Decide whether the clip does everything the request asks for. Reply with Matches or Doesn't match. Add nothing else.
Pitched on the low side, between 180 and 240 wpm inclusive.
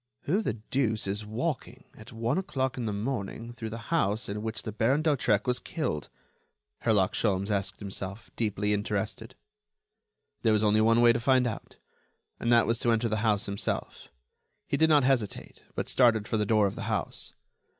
Matches